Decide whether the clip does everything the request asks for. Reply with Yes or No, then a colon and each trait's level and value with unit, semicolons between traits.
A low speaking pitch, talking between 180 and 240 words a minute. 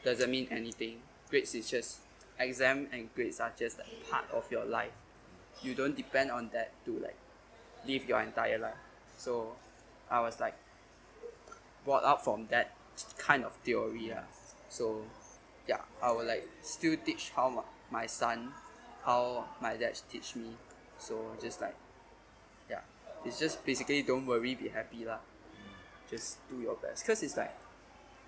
No: low, 130 Hz; average, 155 wpm